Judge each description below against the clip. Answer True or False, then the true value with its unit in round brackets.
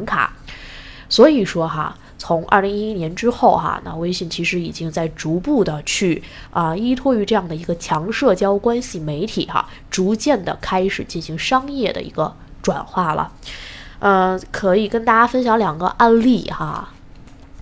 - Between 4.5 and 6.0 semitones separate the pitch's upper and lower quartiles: True (5.2 semitones)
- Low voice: False (190 Hz)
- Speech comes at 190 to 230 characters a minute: False (245 characters per minute)